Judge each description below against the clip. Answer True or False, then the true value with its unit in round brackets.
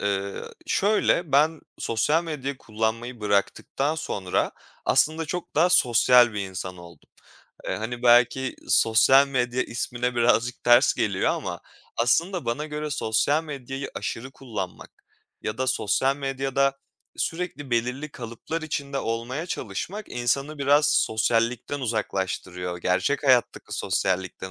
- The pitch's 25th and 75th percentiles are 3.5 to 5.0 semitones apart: True (4.4 semitones)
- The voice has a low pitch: True (125 Hz)